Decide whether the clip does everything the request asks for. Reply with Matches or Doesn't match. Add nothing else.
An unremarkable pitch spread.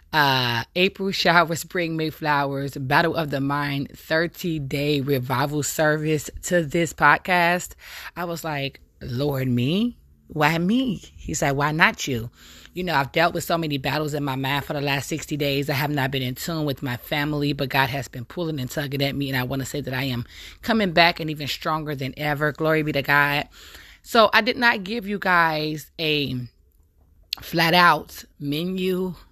Matches